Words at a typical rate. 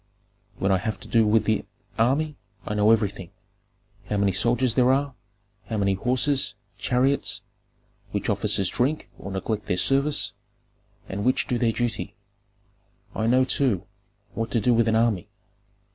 Yes: average, 155 wpm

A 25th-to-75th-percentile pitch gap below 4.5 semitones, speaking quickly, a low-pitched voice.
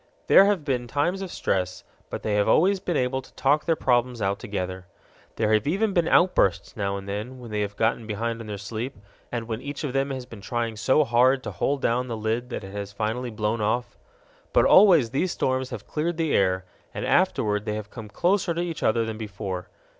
No: average, 5.0 semitones; fast, 220 wpm; low, 120 Hz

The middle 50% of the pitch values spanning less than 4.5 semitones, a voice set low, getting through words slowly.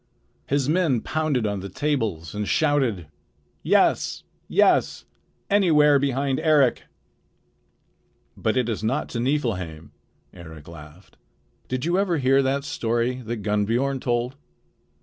No: wide, 5.4 semitones; low, 125 Hz; slow, 120 wpm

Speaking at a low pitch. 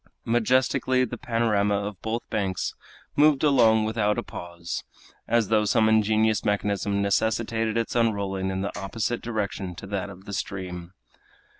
Yes: low, 105 Hz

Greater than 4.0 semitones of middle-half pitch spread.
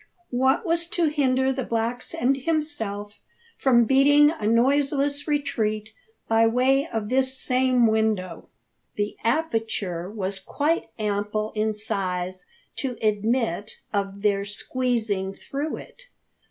Yes: average, 4.6 semitones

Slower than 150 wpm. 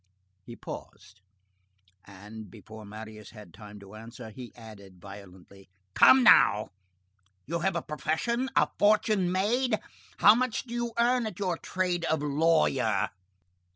Yes: slow, 135 wpm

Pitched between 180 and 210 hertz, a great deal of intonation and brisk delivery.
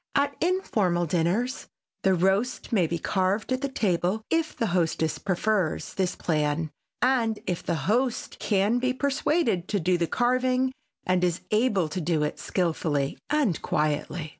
No: high, 190 Hz; wide, 6.7 semitones; average, 155 wpm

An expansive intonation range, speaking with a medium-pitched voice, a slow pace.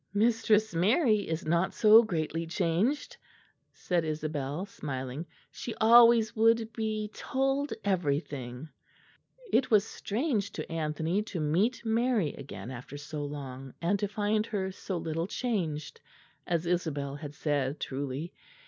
Yes: wide, 6.6 semitones; medium, 175 Hz; slow, 130 wpm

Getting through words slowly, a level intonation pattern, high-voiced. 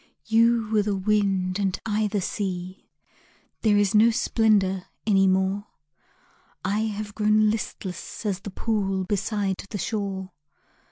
Yes: slow, 130 wpm; narrow, 2.0 semitones; high, 205 Hz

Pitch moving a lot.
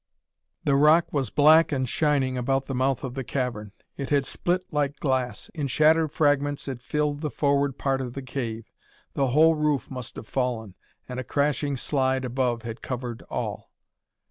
No: narrow, 2.6 semitones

